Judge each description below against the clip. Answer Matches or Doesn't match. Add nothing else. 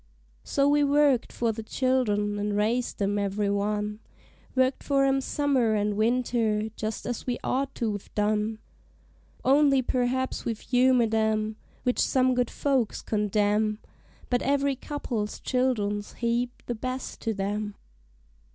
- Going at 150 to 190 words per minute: Doesn't match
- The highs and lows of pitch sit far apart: Doesn't match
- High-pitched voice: Matches